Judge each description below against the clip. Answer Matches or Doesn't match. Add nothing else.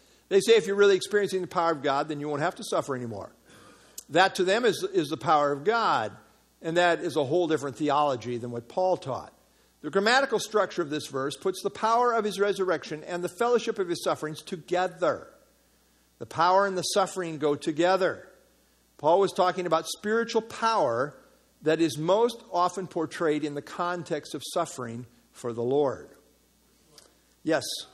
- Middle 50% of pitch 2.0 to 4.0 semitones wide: Doesn't match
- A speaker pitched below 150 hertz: Doesn't match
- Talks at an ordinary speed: Matches